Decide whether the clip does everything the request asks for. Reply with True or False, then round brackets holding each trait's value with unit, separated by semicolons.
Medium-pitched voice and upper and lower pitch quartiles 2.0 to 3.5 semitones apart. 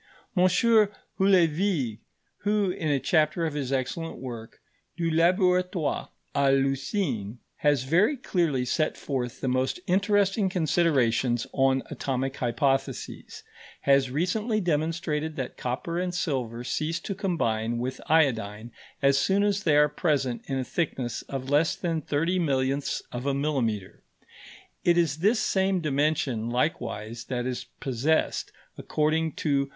False (145 Hz; 5.1 semitones)